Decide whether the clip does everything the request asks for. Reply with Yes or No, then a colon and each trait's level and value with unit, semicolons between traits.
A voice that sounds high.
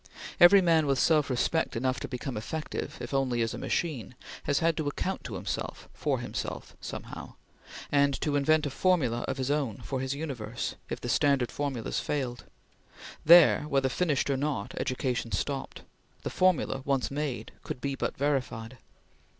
No: medium, 140 Hz